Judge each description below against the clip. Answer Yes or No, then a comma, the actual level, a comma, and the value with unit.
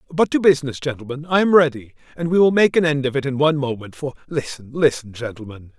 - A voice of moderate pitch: Yes, medium, 145 Hz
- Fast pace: Yes, fast, 230 wpm